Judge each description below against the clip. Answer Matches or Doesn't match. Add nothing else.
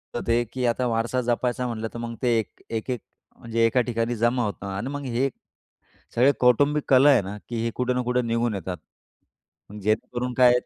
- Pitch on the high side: Doesn't match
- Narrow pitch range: Matches